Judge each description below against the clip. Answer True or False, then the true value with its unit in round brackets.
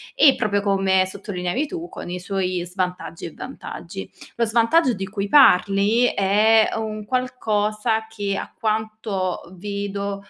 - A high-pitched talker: True (205 Hz)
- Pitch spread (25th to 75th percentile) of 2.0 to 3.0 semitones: True (2.4 semitones)